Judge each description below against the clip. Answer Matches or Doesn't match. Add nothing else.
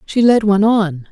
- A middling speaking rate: Doesn't match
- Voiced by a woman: Matches